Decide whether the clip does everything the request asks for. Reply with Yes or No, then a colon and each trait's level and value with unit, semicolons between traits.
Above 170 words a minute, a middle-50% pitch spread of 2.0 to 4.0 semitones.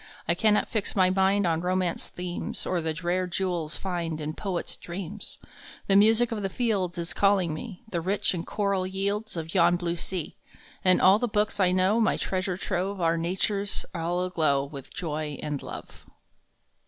Yes: average, 180 wpm; average, 2.8 semitones